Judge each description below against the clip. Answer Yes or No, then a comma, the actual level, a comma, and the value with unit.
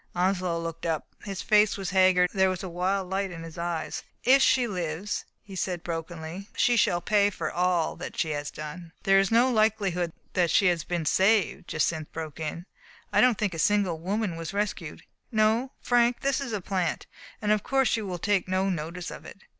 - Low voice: No, medium, 185 Hz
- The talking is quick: Yes, fast, 210 wpm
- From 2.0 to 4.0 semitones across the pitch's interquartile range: Yes, average, 3.6 semitones